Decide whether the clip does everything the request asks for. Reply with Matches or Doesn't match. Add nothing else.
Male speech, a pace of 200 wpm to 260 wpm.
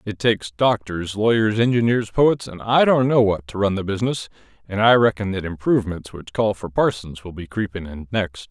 Matches